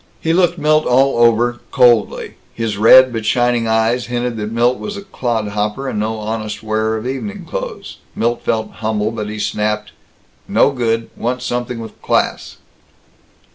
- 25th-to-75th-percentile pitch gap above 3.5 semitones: No, narrow, 2.5 semitones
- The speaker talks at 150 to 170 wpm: Yes, average, 160 wpm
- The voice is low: Yes, low, 115 Hz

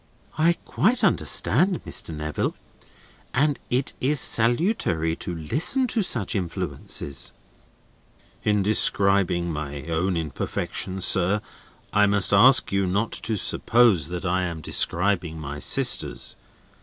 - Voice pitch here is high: No, very low, 95 Hz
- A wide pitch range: Yes, wide, 6.2 semitones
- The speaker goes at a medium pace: No, slow, 120 wpm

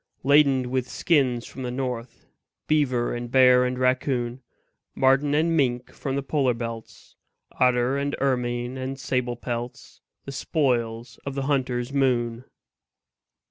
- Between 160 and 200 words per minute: No, slow, 135 wpm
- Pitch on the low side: Yes, low, 130 Hz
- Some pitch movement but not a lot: No, narrow, 2.0 semitones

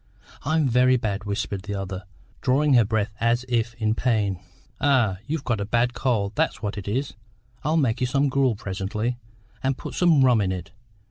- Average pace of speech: Yes, average, 190 wpm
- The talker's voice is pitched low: Yes, low, 120 Hz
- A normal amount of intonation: Yes, average, 4.3 semitones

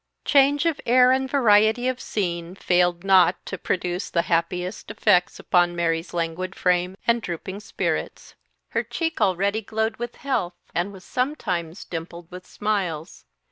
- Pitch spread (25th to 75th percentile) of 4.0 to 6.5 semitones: Yes, average, 4.4 semitones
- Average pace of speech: Yes, average, 145 wpm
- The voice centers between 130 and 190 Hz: Yes, medium, 185 Hz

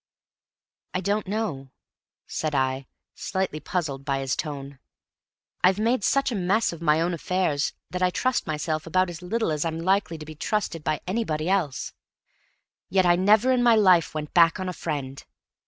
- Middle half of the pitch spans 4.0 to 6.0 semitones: Yes, average, 4.3 semitones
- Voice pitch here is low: No, medium, 175 Hz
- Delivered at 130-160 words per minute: No, average, 175 wpm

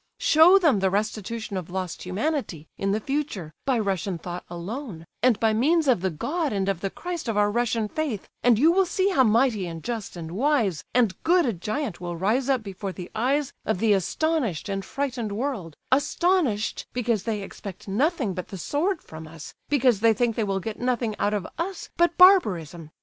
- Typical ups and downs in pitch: No, wide, 6.6 semitones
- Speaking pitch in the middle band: No, high, 220 Hz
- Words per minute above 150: Yes, average, 200 wpm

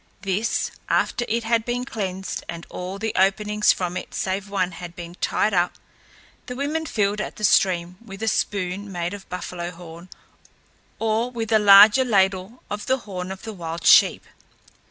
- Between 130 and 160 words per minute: No, average, 175 wpm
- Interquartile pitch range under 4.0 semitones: Yes, average, 3.5 semitones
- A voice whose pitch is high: Yes, high, 200 Hz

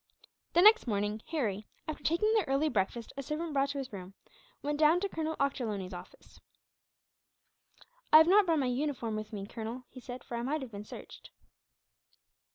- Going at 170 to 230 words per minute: Yes, average, 180 wpm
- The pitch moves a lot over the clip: Yes, wide, 6.4 semitones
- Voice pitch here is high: Yes, very high, 270 Hz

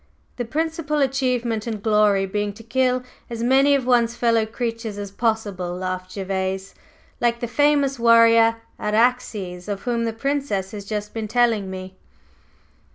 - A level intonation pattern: No, average, 3.4 semitones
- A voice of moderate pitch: No, high, 230 Hz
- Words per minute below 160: Yes, average, 150 wpm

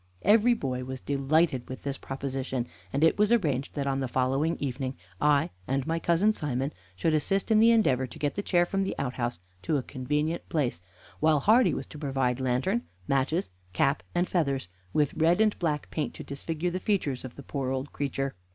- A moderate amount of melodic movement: Yes, average, 4.4 semitones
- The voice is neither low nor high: Yes, medium, 145 Hz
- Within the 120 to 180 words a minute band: No, average, 195 wpm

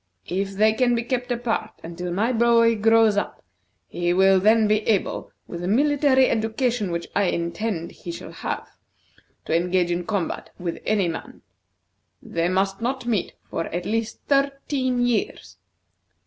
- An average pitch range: Yes, average, 4.9 semitones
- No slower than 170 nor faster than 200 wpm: No, average, 155 wpm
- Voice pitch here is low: No, high, 215 Hz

